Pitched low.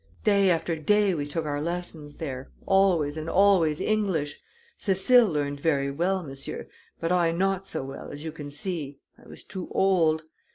No: medium, 165 Hz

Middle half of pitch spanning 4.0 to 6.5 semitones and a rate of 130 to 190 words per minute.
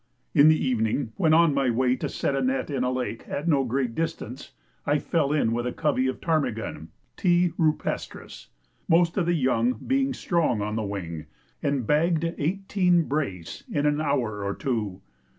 Yes: average, 5.3 semitones; average, 180 wpm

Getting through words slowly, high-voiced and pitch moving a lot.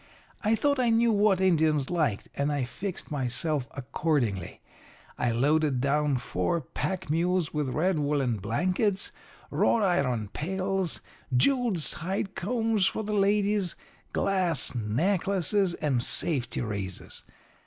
No: slow, 120 wpm; medium, 165 Hz; wide, 6.6 semitones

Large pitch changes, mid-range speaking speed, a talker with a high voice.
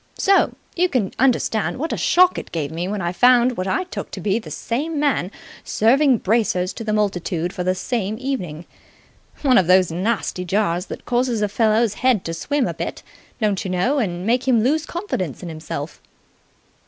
Yes: wide, 5.8 semitones; average, 190 wpm; high, 215 Hz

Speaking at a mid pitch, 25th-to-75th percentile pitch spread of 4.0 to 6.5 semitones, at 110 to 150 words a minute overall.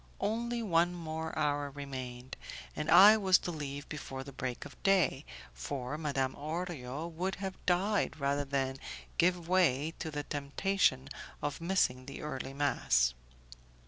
Yes: medium, 150 Hz; average, 4.6 semitones; average, 145 wpm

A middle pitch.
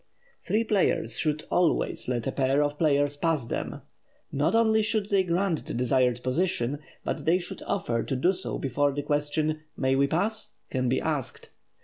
Yes: medium, 145 Hz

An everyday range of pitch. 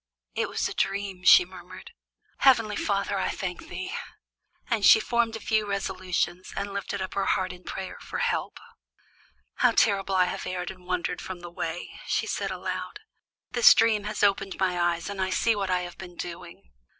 No: narrow, 2.2 semitones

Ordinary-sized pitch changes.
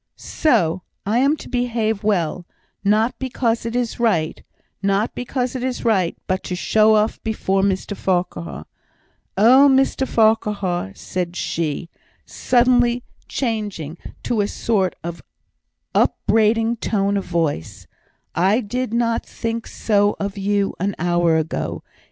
Yes: average, 4.2 semitones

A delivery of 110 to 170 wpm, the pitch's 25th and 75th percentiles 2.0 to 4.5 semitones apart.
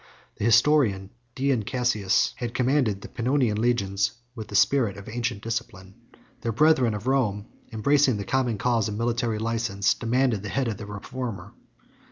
Yes: average, 160 wpm; average, 3.4 semitones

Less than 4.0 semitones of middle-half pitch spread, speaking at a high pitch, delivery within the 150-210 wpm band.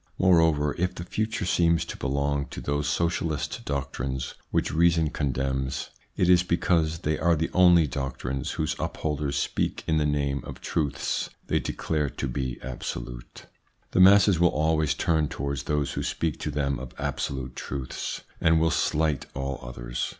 No: average, 3.4 semitones; very low, 75 Hz; average, 160 wpm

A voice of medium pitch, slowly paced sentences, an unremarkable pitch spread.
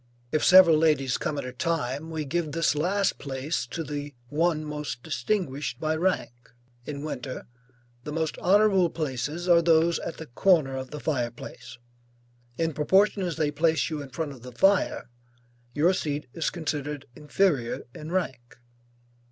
No: medium, 155 Hz; average, 160 wpm; average, 3.3 semitones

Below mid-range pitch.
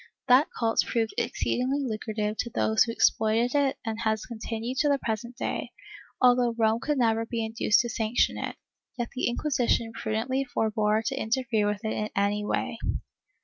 No: high, 230 Hz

